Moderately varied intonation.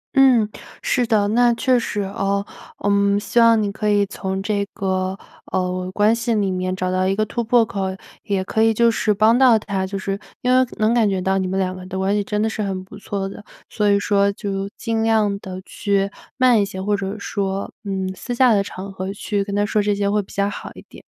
No: narrow, 2.1 semitones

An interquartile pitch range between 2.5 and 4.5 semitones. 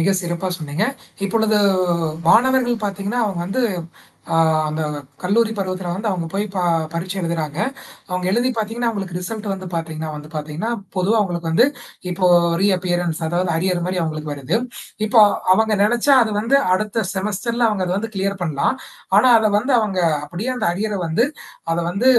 Yes: average, 4.2 semitones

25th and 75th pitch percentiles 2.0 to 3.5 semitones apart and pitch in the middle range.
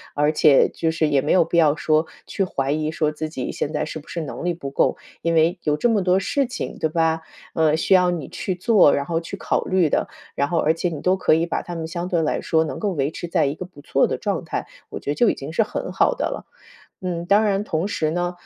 Yes: average, 2.8 semitones; medium, 165 Hz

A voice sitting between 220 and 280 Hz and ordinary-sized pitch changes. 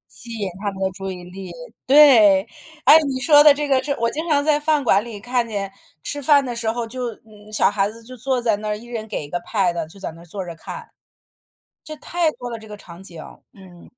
No: high, 225 Hz; wide, 5.9 semitones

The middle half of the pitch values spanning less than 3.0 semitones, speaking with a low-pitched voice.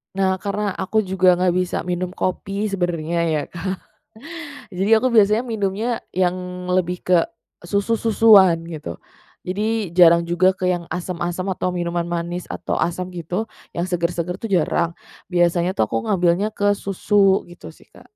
No: narrow, 2.4 semitones; medium, 180 Hz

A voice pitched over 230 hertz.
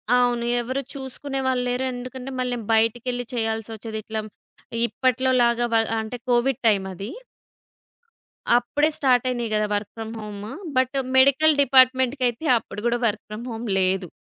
Yes: high, 245 Hz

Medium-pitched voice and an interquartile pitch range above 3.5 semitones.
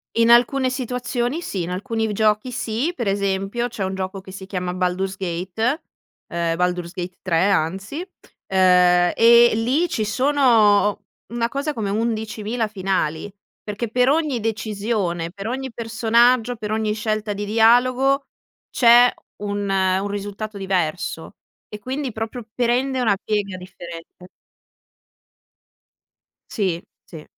No: high, 215 Hz; average, 4.0 semitones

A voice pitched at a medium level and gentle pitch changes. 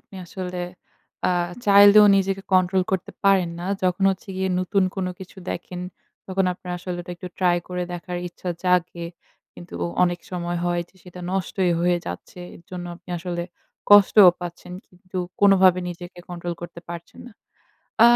Yes: medium, 180 Hz; narrow, 1.4 semitones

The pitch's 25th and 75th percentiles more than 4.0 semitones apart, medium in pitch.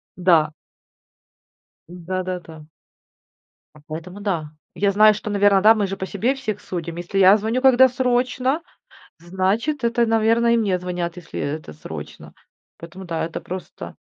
No: average, 4.5 semitones; high, 195 Hz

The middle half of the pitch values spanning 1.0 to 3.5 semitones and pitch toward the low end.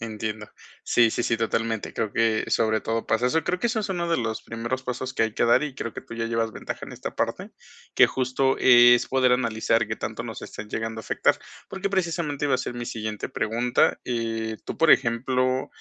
Yes: narrow, 2.6 semitones; low, 115 Hz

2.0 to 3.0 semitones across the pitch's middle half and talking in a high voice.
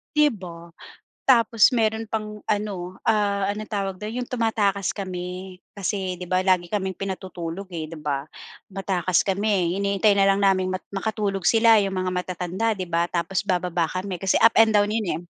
Yes: narrow, 2.6 semitones; high, 195 Hz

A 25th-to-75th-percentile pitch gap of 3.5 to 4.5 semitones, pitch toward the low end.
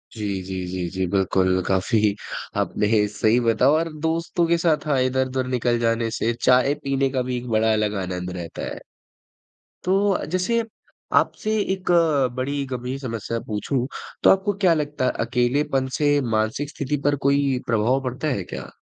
No: average, 5.0 semitones; low, 125 Hz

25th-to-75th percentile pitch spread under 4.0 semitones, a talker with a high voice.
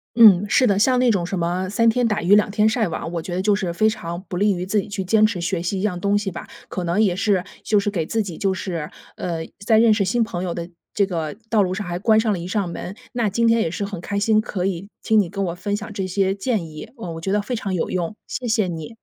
Yes: average, 3.4 semitones; high, 195 Hz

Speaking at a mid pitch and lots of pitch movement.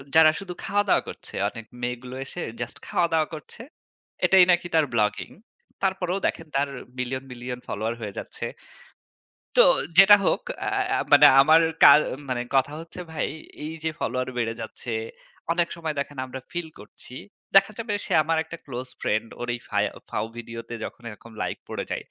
Yes: medium, 145 Hz; wide, 5.8 semitones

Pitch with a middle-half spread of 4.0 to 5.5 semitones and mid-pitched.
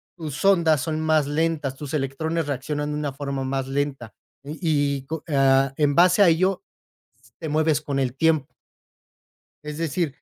No: average, 2.7 semitones; medium, 150 Hz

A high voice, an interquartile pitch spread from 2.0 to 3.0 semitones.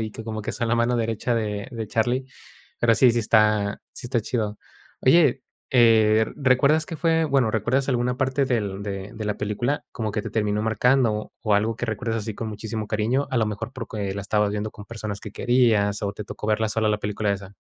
No: low, 110 Hz; narrow, 2.6 semitones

